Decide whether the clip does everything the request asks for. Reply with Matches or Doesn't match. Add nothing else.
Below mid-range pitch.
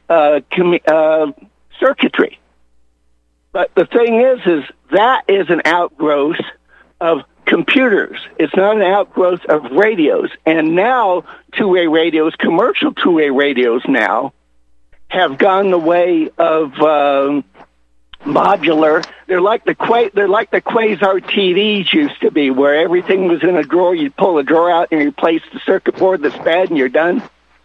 Doesn't match